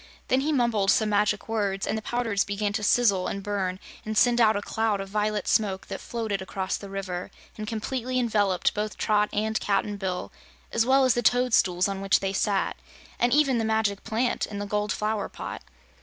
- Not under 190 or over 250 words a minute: Yes, average, 200 wpm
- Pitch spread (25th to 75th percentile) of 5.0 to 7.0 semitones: No, narrow, 2.4 semitones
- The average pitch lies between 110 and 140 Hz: No, high, 210 Hz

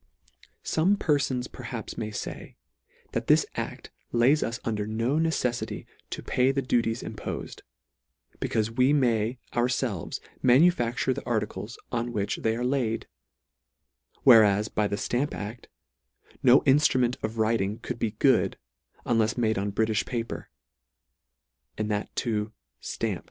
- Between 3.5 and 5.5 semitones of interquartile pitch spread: No, average, 2.8 semitones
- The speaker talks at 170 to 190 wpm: No, average, 140 wpm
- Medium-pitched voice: No, low, 120 Hz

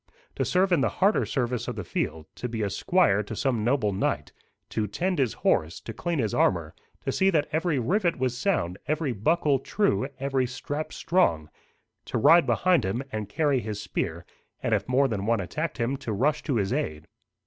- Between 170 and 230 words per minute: Yes, average, 200 wpm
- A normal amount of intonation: No, wide, 6.5 semitones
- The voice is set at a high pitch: No, low, 130 Hz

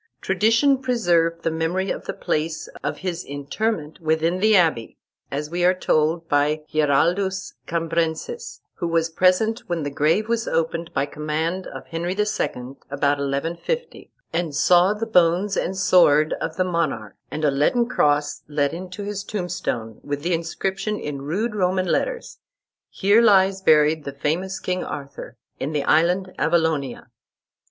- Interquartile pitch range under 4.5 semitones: Yes, average, 4.0 semitones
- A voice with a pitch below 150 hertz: No, medium, 170 Hz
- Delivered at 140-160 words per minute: Yes, average, 150 wpm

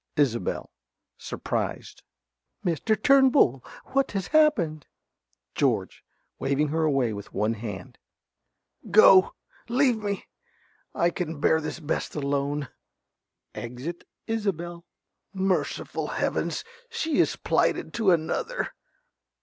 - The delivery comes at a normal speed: No, slow, 100 wpm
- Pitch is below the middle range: No, medium, 170 Hz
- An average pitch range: No, wide, 7.4 semitones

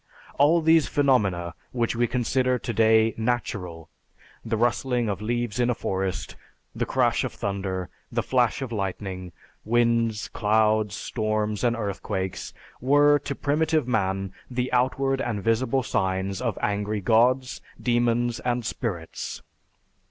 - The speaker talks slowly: Yes, slow, 130 wpm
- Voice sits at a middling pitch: No, low, 115 Hz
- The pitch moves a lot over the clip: No, average, 3.6 semitones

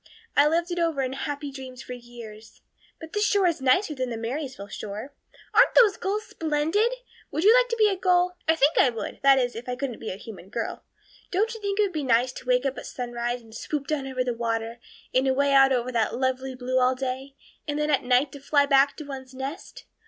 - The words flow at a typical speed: No, fast, 235 wpm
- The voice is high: Yes, very high, 270 Hz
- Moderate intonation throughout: Yes, average, 4.2 semitones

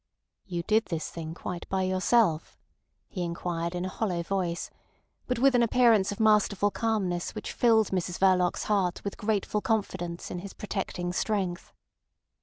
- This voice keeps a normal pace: Yes, average, 155 wpm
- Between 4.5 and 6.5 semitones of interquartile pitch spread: No, average, 3.4 semitones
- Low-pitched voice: No, high, 190 Hz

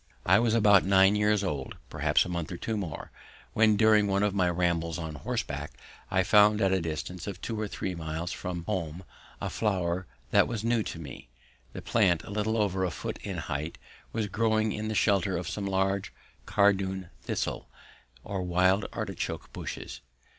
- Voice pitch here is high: No, very low, 95 Hz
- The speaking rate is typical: Yes, average, 180 wpm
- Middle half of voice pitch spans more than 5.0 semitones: No, average, 3.2 semitones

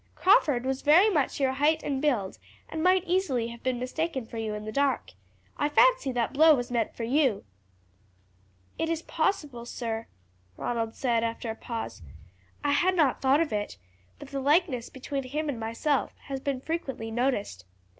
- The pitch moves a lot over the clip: No, average, 4.6 semitones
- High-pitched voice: Yes, very high, 265 Hz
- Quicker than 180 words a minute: No, average, 175 wpm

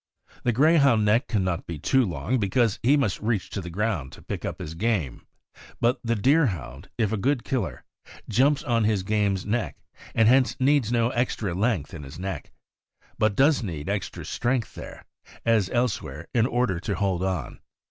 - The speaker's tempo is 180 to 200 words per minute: Yes, average, 185 wpm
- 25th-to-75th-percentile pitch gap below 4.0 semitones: No, average, 4.6 semitones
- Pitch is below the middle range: Yes, low, 110 Hz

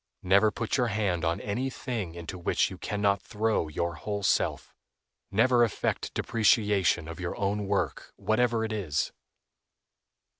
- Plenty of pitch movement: No, average, 3.8 semitones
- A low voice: Yes, low, 100 Hz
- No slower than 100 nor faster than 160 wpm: Yes, average, 150 wpm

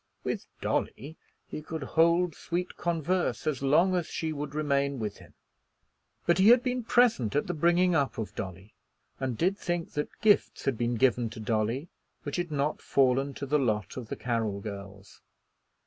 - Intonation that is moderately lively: No, wide, 6.4 semitones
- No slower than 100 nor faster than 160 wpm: No, average, 180 wpm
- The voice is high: No, medium, 145 Hz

